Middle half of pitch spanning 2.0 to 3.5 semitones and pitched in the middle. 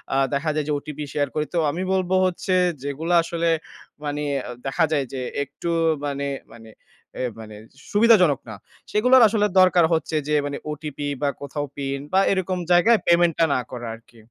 No: average, 4.2 semitones; medium, 155 Hz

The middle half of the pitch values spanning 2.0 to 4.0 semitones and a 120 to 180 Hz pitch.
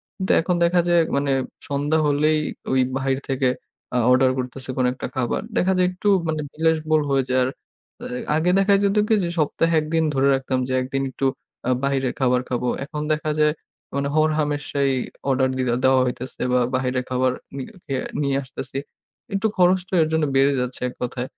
Yes: average, 3.5 semitones; medium, 140 Hz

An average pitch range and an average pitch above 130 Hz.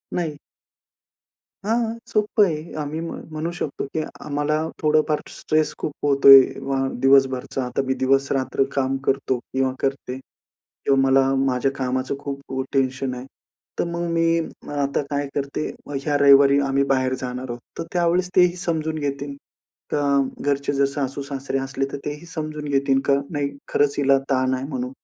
No: narrow, 2.2 semitones; medium, 140 Hz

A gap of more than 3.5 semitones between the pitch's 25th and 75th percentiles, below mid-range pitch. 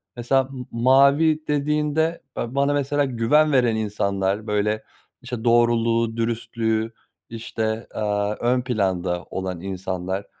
Yes: average, 4.2 semitones; low, 115 Hz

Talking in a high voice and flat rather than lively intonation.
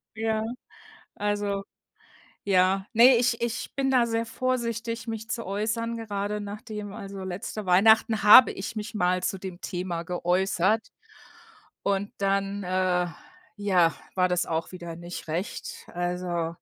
No: high, 200 Hz; average, 3.5 semitones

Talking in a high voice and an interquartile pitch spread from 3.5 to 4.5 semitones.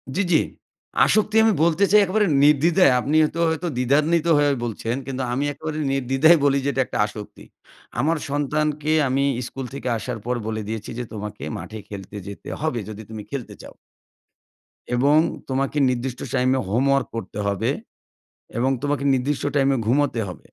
No: low, 135 Hz; average, 4.0 semitones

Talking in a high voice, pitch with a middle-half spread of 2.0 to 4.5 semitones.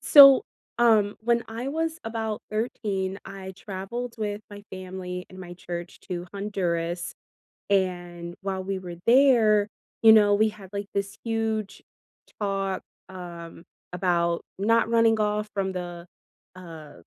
Yes: high, 195 Hz; average, 3.4 semitones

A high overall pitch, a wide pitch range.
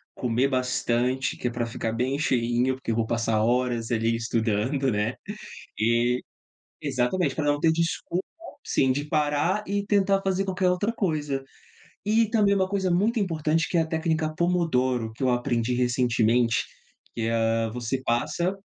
No: low, 130 Hz; wide, 6.5 semitones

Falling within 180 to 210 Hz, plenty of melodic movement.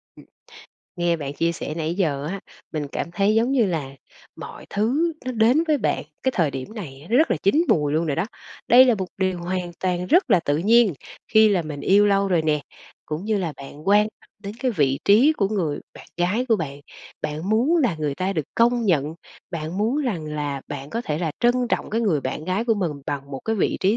Yes: medium, 185 Hz; wide, 6.4 semitones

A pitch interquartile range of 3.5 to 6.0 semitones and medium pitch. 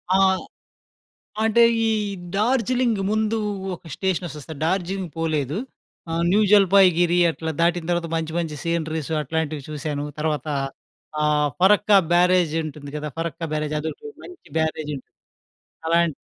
Yes: average, 3.9 semitones; medium, 165 Hz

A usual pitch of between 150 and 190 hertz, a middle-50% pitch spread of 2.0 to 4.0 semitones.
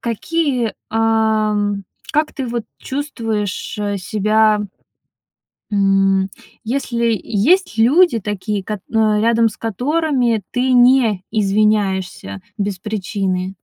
No: high, 220 Hz; average, 2.9 semitones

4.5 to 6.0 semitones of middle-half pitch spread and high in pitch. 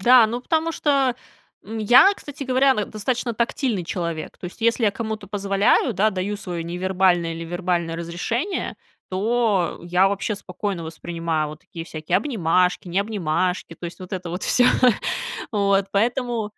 Yes: average, 4.8 semitones; high, 195 Hz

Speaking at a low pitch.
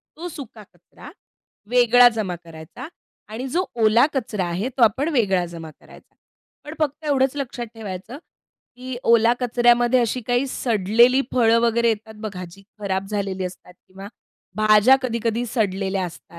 No: high, 230 Hz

